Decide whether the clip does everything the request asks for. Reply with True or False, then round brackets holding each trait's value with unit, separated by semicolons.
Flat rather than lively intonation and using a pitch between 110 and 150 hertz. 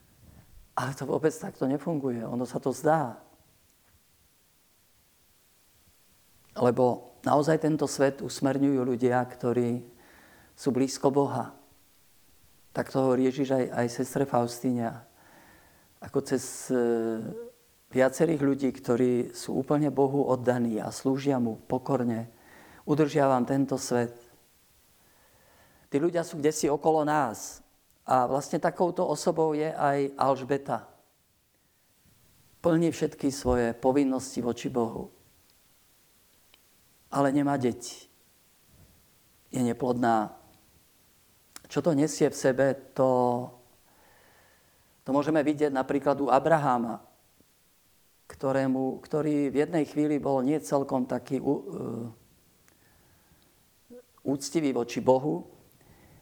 False (3.1 semitones; 135 Hz)